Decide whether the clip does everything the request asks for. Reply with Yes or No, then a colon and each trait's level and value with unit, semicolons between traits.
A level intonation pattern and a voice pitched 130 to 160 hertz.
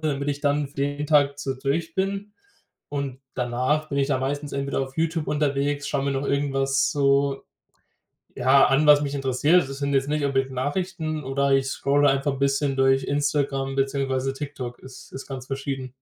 Yes: narrow, 1.3 semitones; medium, 140 Hz